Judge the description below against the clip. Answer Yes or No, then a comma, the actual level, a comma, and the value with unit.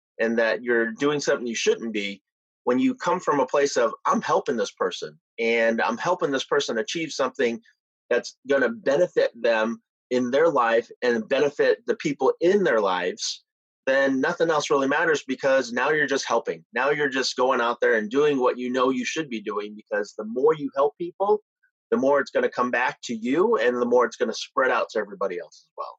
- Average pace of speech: No, fast, 210 wpm